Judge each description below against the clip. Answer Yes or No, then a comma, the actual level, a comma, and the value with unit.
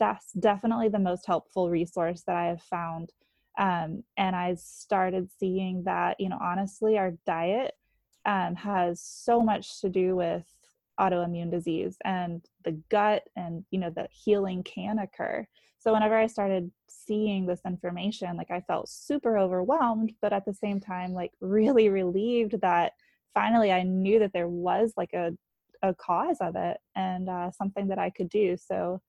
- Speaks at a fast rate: No, average, 165 wpm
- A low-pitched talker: No, high, 190 Hz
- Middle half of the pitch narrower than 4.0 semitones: Yes, average, 2.9 semitones